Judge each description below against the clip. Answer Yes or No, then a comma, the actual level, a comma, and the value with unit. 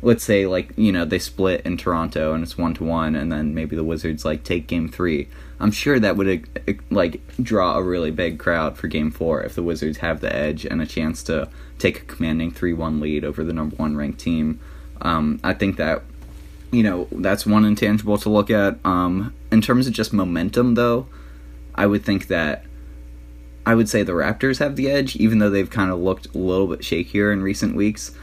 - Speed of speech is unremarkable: No, fast, 215 wpm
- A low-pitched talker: Yes, very low, 85 Hz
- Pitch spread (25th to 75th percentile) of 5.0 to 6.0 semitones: Yes, average, 5.3 semitones